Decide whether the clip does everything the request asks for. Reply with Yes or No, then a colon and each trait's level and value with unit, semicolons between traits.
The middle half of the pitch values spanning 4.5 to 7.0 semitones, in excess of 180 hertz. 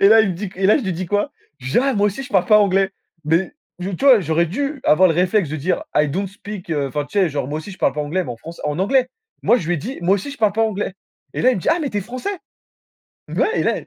Yes: average, 4.8 semitones; high, 190 Hz